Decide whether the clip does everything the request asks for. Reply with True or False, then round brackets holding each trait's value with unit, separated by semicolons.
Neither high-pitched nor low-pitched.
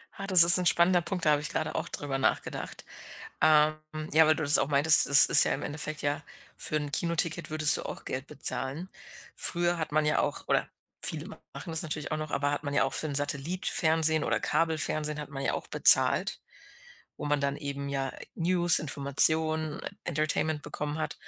True (155 Hz)